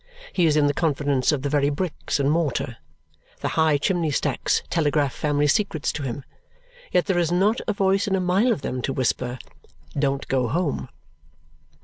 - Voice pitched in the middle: Yes, medium, 150 Hz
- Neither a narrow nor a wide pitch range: Yes, average, 4.2 semitones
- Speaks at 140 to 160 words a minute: No, average, 180 wpm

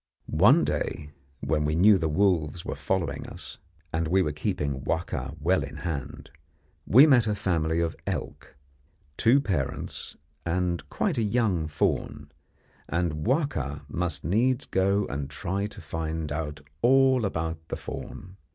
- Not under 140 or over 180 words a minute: Yes, average, 145 wpm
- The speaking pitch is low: Yes, very low, 85 Hz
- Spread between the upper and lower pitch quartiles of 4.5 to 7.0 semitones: Yes, average, 5.1 semitones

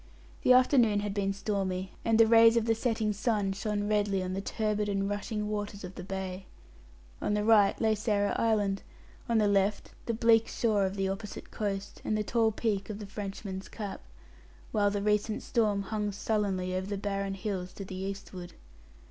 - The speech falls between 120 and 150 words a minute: No, average, 180 wpm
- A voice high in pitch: Yes, high, 205 Hz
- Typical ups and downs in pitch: No, narrow, 1.8 semitones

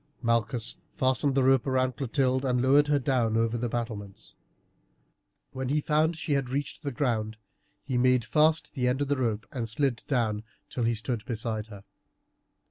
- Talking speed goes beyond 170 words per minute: Yes, average, 180 wpm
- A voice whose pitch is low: Yes, low, 125 Hz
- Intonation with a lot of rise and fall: No, average, 3.2 semitones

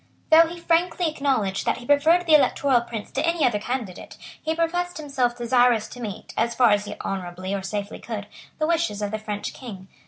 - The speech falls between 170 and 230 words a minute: Yes, average, 200 wpm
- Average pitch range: No, wide, 7.2 semitones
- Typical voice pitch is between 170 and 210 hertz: No, high, 245 Hz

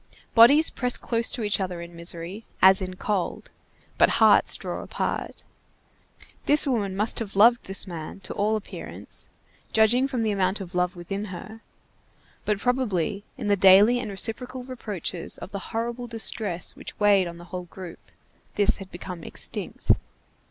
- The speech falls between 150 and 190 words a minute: Yes, average, 160 wpm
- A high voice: Yes, high, 205 Hz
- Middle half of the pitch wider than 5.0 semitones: No, average, 3.7 semitones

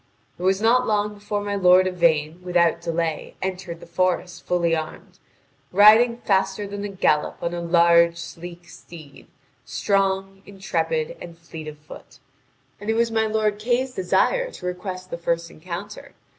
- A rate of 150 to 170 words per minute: Yes, average, 155 wpm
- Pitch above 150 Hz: Yes, medium, 185 Hz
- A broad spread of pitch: No, average, 3.3 semitones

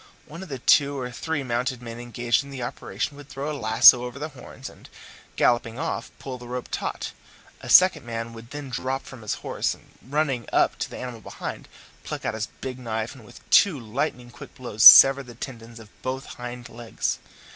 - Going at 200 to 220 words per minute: Yes, fast, 205 wpm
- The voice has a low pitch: Yes, low, 125 Hz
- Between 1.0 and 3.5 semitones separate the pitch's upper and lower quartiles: Yes, average, 2.8 semitones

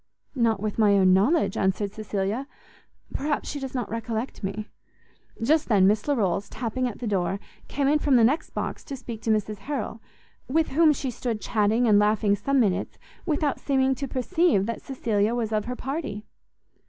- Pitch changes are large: No, average, 4.6 semitones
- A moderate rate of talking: Yes, average, 180 wpm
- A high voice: Yes, high, 230 Hz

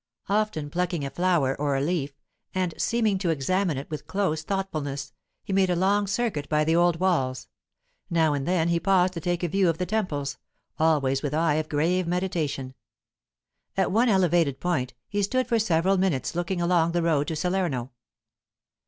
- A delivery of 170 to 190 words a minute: Yes, average, 180 wpm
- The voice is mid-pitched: Yes, medium, 170 Hz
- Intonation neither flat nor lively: Yes, average, 4.1 semitones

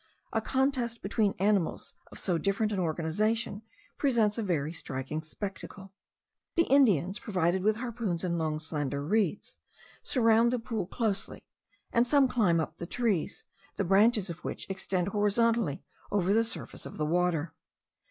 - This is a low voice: No, high, 200 Hz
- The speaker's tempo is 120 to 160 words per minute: Yes, average, 150 wpm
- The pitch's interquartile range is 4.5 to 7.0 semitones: Yes, average, 5.0 semitones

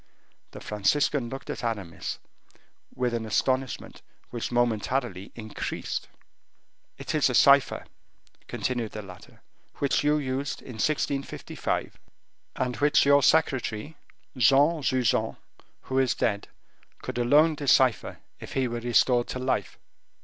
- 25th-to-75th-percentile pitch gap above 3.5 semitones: No, average, 3.2 semitones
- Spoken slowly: Yes, slow, 120 wpm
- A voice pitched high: No, low, 125 Hz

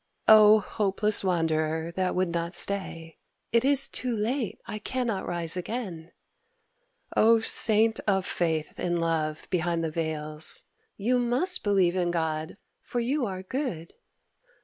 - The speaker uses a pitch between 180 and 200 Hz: Yes, medium, 185 Hz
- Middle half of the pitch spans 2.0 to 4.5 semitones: No, average, 5.2 semitones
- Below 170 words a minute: Yes, slow, 135 wpm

